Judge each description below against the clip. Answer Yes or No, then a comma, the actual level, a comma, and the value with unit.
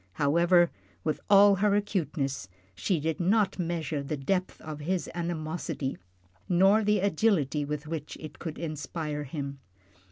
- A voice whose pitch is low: No, medium, 165 Hz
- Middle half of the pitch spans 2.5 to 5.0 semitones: Yes, average, 4.0 semitones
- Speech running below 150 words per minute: Yes, slow, 135 wpm